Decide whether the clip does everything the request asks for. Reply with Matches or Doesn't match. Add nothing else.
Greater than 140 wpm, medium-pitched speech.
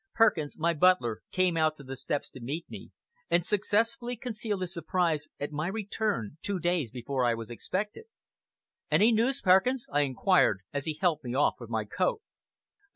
Matches